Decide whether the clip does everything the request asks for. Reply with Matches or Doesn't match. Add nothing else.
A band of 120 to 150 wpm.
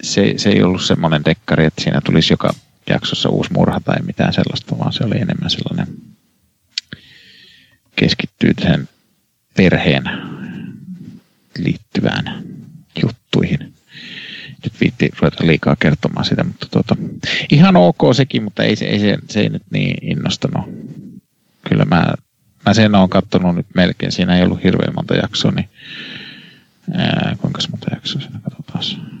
Matches